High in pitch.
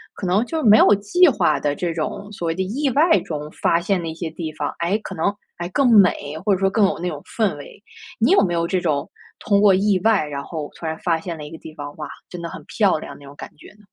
No: medium, 180 Hz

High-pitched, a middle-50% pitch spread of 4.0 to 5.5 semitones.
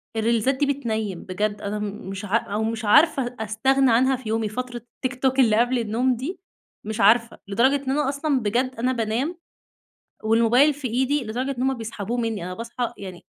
No: high, 235 Hz; average, 3.3 semitones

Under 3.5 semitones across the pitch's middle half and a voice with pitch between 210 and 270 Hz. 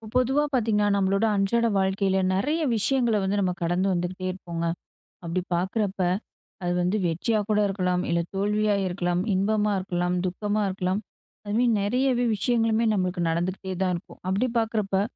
No: average, 3.0 semitones; high, 195 Hz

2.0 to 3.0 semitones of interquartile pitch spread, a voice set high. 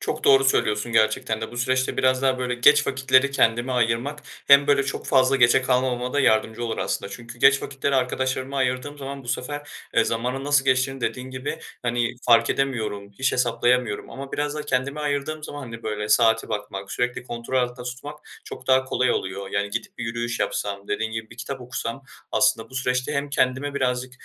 No: narrow, 2.5 semitones; low, 125 Hz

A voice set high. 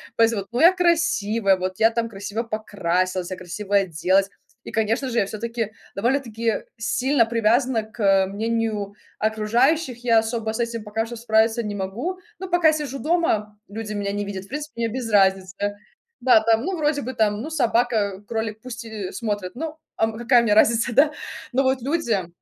Yes: high, 225 Hz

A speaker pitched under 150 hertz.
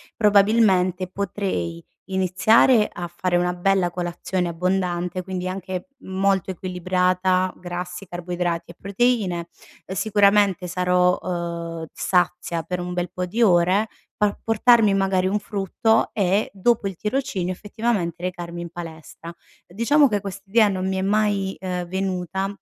No: medium, 185 Hz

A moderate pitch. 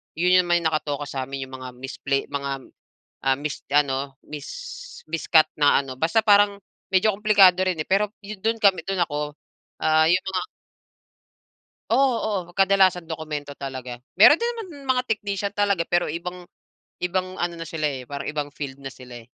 Yes: medium, 165 Hz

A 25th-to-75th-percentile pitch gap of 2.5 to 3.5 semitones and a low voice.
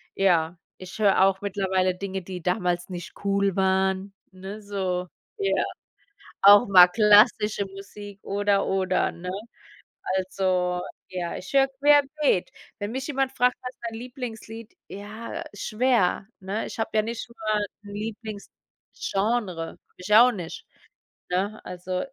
No: average, 3.1 semitones; high, 200 Hz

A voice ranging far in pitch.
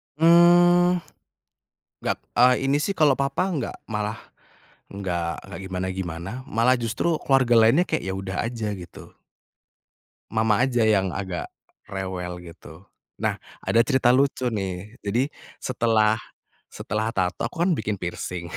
Yes: wide, 5.9 semitones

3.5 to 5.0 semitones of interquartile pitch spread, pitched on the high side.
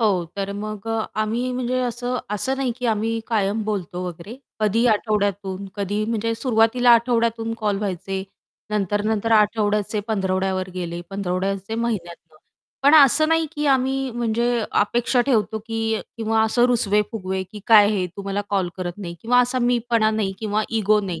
No: average, 3.0 semitones; high, 215 Hz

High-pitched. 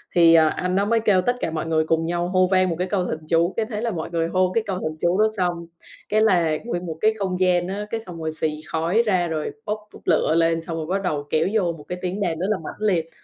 No: medium, 180 Hz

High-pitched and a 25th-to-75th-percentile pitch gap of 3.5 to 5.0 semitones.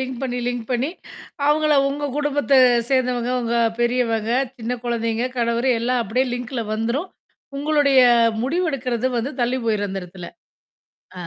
No: high, 245 Hz; average, 2.8 semitones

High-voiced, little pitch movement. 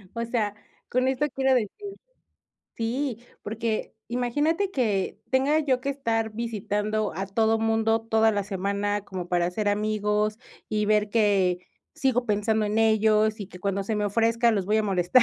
Yes: high, 220 Hz; narrow, 2.3 semitones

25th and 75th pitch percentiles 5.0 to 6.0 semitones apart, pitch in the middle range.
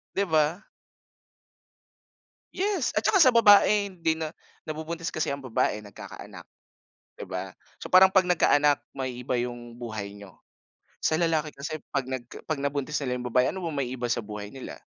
Yes: average, 5.3 semitones; medium, 145 Hz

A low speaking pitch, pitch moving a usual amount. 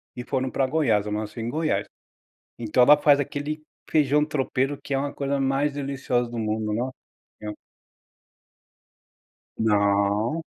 Yes: low, 130 Hz; average, 4.6 semitones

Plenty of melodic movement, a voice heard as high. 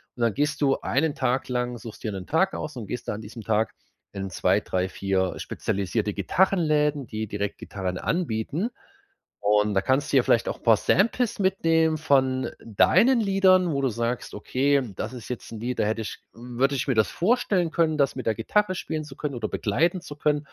No: wide, 6.3 semitones; low, 130 Hz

